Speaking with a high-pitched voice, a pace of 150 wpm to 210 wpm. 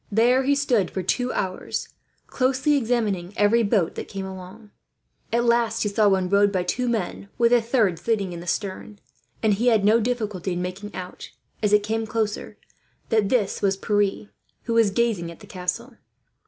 Yes: high, 210 Hz; average, 180 wpm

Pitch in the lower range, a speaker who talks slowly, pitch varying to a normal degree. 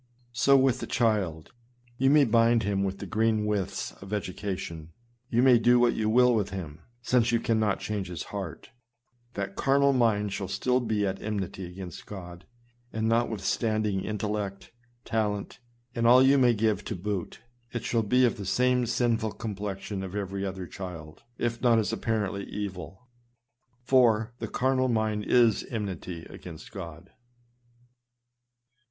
No: low, 105 Hz; average, 160 wpm; average, 3.5 semitones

